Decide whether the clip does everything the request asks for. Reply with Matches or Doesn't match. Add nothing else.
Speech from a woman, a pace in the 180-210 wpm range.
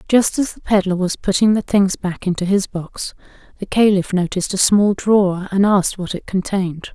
Matches